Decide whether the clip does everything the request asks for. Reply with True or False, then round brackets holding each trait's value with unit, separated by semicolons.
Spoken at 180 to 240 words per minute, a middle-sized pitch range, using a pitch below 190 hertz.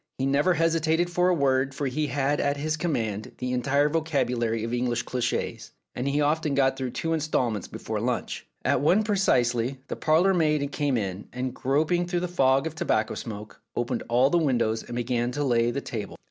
True (195 wpm; 4.4 semitones; 135 Hz)